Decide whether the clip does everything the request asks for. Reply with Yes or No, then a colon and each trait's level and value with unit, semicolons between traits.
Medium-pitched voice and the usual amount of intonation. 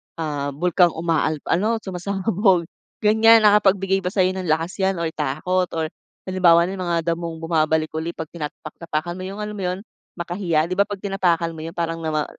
Yes: medium, 175 Hz; average, 3.0 semitones